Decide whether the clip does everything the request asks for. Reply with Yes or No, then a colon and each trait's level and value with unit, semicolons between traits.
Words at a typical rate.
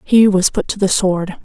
No: fast, 250 wpm